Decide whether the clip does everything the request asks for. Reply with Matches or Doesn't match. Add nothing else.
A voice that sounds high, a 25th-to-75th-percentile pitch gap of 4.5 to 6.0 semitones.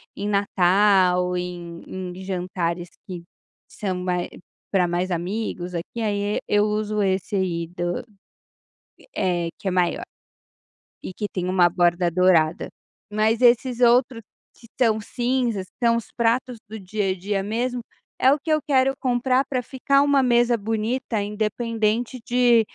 Matches